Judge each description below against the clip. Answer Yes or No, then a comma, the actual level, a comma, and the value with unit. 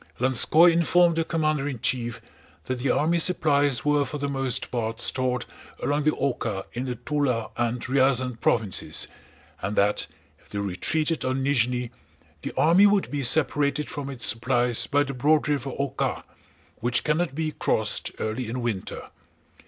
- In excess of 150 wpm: Yes, average, 160 wpm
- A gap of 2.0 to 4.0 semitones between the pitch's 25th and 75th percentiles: Yes, average, 3.7 semitones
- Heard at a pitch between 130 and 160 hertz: Yes, low, 135 Hz